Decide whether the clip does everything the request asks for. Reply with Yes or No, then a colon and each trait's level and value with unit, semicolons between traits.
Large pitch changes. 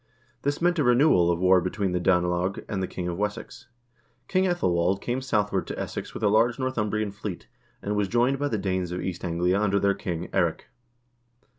No: average, 5.0 semitones